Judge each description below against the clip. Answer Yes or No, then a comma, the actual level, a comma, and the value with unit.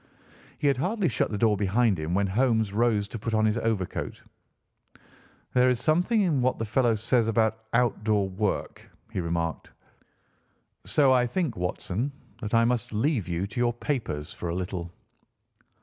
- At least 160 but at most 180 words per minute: Yes, average, 165 wpm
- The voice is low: Yes, low, 110 Hz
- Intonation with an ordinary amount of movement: Yes, average, 4.0 semitones